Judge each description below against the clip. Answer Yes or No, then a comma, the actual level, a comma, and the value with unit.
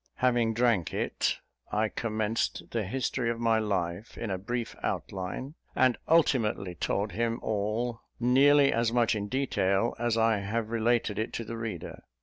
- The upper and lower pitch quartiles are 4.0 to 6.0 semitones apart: No, narrow, 2.4 semitones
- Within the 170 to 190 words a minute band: No, average, 155 wpm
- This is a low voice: Yes, low, 115 Hz